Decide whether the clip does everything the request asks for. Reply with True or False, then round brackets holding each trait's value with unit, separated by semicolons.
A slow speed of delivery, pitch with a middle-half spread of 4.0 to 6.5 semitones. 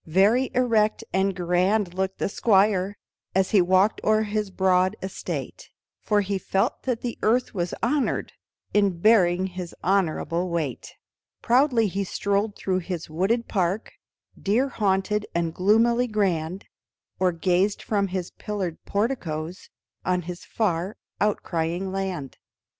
False (130 wpm; 3.0 semitones)